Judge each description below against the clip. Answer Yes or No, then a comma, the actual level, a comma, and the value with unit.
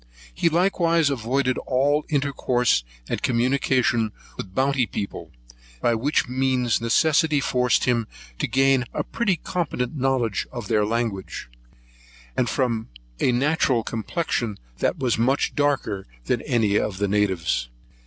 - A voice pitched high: No, low, 125 Hz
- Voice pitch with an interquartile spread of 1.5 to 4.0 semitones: Yes, average, 3.6 semitones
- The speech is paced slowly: Yes, slow, 125 wpm